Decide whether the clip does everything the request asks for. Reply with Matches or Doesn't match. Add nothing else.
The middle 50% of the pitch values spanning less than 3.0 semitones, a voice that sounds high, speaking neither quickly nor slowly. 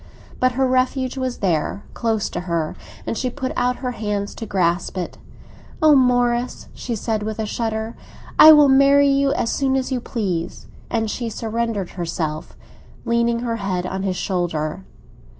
Doesn't match